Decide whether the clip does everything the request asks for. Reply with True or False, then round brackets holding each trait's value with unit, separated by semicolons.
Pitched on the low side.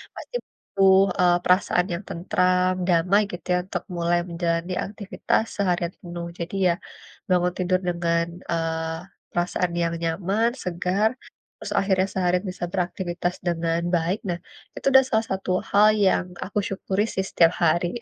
False (180 Hz)